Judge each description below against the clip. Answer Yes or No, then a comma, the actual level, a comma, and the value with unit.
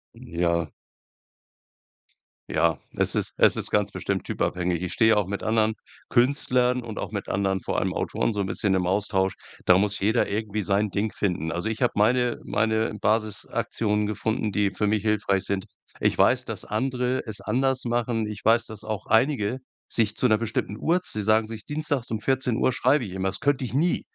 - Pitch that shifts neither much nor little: Yes, average, 3.2 semitones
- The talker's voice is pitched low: Yes, low, 110 Hz